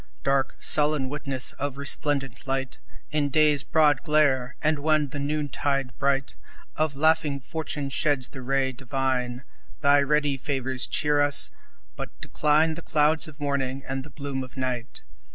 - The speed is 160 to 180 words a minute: No, average, 150 wpm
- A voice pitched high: No, medium, 140 Hz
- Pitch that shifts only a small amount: Yes, narrow, 2.0 semitones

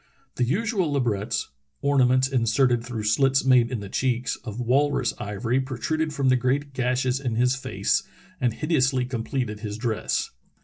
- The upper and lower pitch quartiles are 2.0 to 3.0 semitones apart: Yes, narrow, 2.6 semitones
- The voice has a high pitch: No, low, 125 Hz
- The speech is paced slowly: No, average, 150 wpm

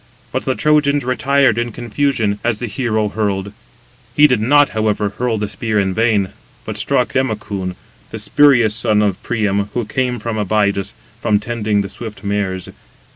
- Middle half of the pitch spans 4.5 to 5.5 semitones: No, average, 3.1 semitones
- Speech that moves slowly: No, average, 165 wpm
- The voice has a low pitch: Yes, low, 110 Hz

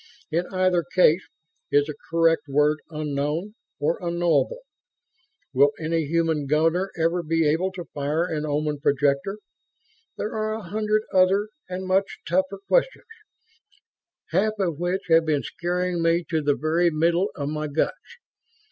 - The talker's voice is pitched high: No, medium, 165 Hz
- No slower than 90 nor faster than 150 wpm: Yes, average, 145 wpm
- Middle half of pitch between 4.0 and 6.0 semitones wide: No, average, 3.4 semitones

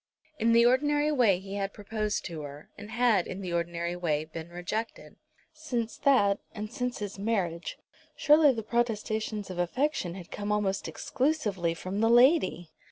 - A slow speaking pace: No, average, 165 wpm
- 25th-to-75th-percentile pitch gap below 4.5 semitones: No, average, 5.3 semitones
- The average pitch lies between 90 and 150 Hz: No, high, 210 Hz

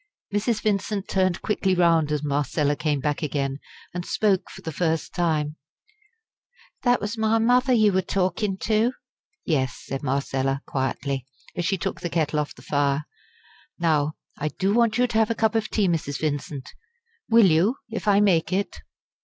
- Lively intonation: Yes, wide, 6.2 semitones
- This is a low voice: No, medium, 175 Hz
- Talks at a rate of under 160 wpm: No, average, 170 wpm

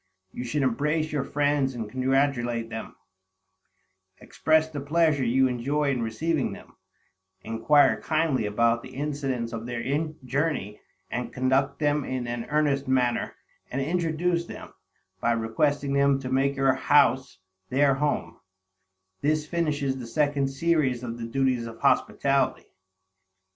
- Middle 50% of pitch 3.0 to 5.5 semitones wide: Yes, average, 3.3 semitones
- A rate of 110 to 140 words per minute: Yes, slow, 135 wpm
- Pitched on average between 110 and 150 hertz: Yes, low, 135 Hz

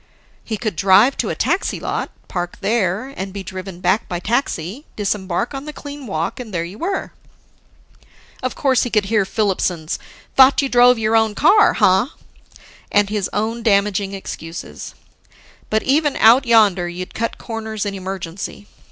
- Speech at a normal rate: Yes, average, 160 wpm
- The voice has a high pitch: Yes, high, 210 Hz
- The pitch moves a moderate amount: Yes, average, 4.1 semitones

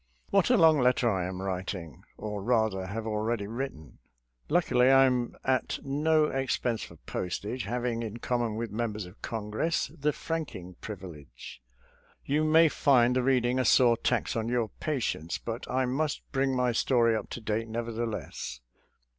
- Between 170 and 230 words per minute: Yes, average, 175 wpm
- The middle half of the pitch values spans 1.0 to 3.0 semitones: No, average, 3.7 semitones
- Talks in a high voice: No, low, 120 Hz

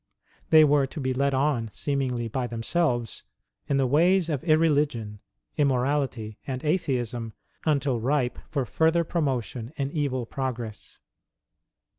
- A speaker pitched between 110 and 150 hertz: Yes, low, 135 Hz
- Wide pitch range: No, average, 3.5 semitones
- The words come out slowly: Yes, slow, 125 wpm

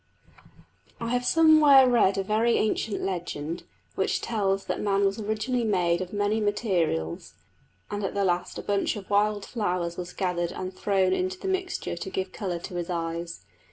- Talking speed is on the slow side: No, average, 180 wpm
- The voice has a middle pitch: No, high, 200 Hz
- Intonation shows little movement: No, average, 3.6 semitones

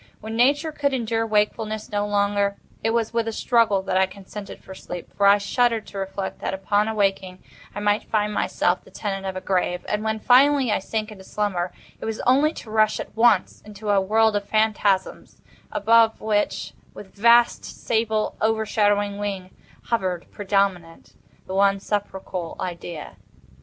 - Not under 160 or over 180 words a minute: Yes, average, 165 wpm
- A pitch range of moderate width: No, narrow, 2.2 semitones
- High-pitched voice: Yes, high, 205 Hz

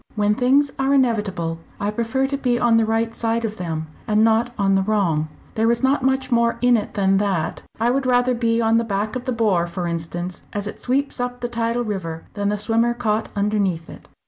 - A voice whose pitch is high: Yes, high, 225 Hz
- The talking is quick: Yes, fast, 225 wpm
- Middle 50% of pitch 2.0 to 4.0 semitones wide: Yes, average, 3.4 semitones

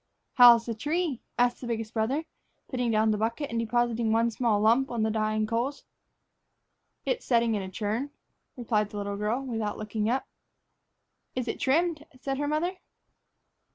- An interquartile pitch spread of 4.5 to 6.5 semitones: No, average, 3.3 semitones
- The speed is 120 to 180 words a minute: Yes, average, 165 wpm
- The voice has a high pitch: Yes, high, 235 Hz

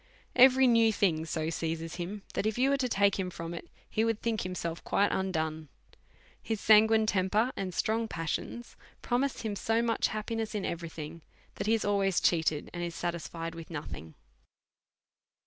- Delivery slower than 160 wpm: No, average, 180 wpm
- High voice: Yes, high, 195 Hz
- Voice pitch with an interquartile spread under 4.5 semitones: No, average, 5.0 semitones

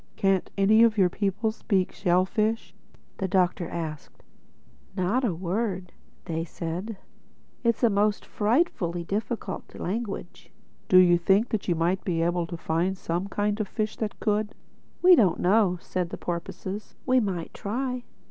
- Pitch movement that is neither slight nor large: Yes, average, 3.5 semitones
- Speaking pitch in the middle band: No, high, 195 Hz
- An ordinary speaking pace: Yes, average, 155 wpm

